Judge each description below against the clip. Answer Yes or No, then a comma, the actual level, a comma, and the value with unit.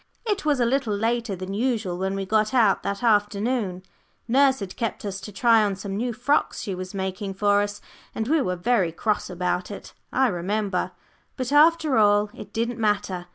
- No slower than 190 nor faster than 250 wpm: Yes, average, 195 wpm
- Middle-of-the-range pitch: No, high, 210 Hz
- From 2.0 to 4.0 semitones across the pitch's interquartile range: Yes, average, 3.7 semitones